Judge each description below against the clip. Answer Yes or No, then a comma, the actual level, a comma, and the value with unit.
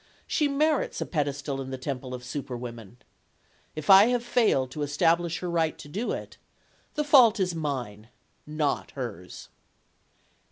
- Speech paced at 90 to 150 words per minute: Yes, average, 145 wpm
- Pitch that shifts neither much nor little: No, wide, 6.9 semitones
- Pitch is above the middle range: No, medium, 150 Hz